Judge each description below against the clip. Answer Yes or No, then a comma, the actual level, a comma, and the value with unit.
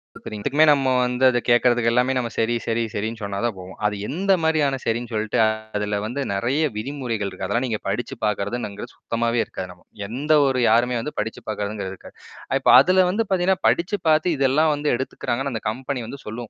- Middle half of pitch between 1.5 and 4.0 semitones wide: No, average, 4.5 semitones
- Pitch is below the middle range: Yes, low, 120 Hz